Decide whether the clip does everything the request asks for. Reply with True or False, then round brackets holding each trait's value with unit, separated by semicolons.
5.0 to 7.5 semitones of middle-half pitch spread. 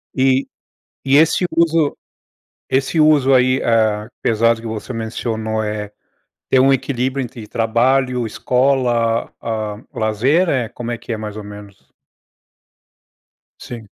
False (3.4 semitones)